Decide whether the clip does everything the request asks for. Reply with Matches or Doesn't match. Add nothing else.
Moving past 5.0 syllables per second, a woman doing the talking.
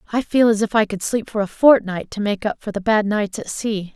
Matches